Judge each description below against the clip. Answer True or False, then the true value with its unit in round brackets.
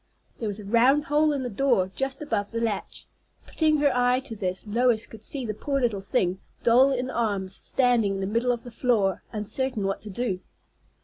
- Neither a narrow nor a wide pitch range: True (4.2 semitones)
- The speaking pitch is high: True (235 Hz)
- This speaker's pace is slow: False (205 wpm)